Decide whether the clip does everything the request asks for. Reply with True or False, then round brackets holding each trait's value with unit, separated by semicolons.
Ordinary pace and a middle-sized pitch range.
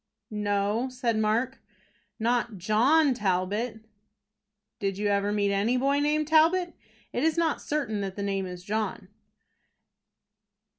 False (130 wpm; 4.9 semitones)